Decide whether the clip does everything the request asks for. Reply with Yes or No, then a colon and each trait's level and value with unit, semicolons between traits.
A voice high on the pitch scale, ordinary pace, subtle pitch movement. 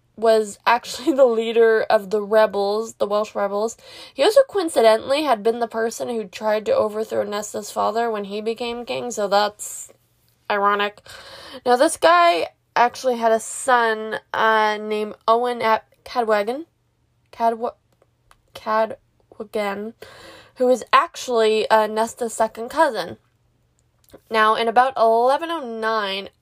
No: high, 225 Hz; slow, 125 wpm; narrow, 2.0 semitones